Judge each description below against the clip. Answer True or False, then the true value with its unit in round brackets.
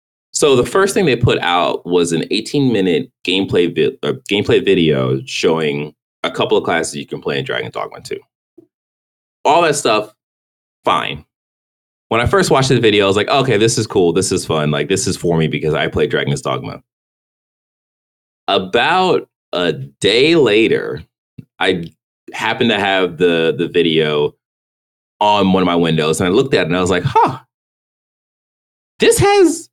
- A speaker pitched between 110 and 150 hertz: False (80 Hz)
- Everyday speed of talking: True (175 wpm)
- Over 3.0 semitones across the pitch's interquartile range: True (5.2 semitones)